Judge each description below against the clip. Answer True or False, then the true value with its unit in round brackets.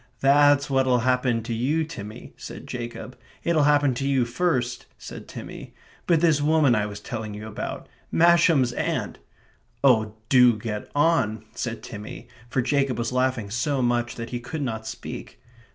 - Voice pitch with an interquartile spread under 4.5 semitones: True (3.8 semitones)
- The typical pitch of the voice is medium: False (125 Hz)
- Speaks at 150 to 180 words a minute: True (165 wpm)